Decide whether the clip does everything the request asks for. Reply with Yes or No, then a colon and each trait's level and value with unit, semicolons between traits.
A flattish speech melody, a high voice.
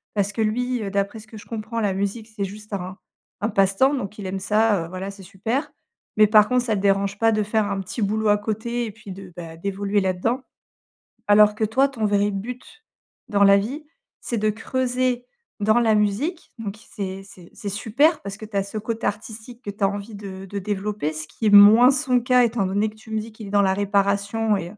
Yes: narrow, 2.2 semitones; high, 210 Hz